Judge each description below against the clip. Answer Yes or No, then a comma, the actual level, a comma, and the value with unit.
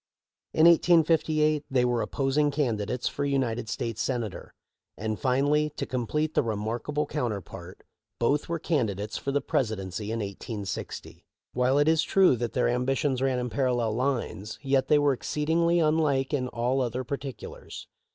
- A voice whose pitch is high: No, low, 130 Hz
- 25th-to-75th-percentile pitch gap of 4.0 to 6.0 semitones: Yes, average, 4.3 semitones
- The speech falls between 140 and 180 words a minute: Yes, average, 150 wpm